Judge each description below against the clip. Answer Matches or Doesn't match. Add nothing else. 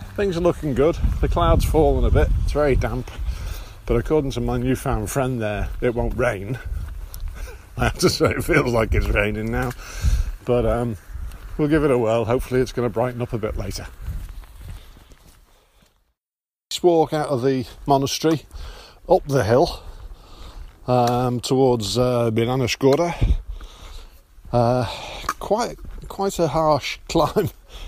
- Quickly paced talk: Doesn't match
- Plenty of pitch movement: Matches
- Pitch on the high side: Doesn't match